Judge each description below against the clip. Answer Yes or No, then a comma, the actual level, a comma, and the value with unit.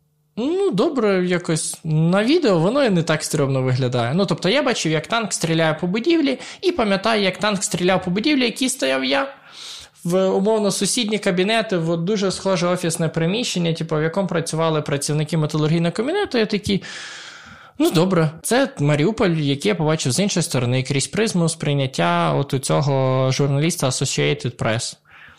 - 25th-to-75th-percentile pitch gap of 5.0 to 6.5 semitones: Yes, wide, 5.4 semitones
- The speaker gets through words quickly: Yes, fast, 160 wpm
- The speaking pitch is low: No, medium, 170 Hz